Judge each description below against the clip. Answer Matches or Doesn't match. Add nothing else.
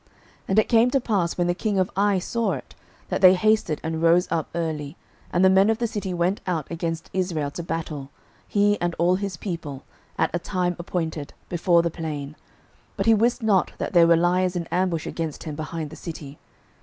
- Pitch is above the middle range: Doesn't match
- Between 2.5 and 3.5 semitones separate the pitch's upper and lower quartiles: Matches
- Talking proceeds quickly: Matches